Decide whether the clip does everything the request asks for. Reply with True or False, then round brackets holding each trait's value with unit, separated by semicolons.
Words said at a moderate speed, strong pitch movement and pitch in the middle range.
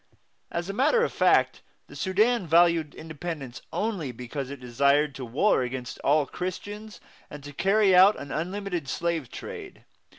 True (155 wpm; 5.9 semitones; 165 Hz)